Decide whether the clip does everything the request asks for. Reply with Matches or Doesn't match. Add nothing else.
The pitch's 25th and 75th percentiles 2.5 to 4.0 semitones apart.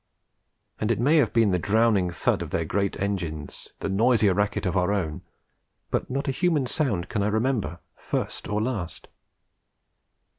Doesn't match